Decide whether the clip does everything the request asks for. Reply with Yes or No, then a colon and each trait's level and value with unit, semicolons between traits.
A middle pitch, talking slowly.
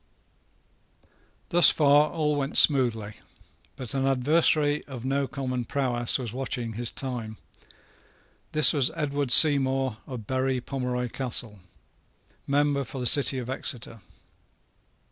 No: low, 130 Hz; slow, 120 wpm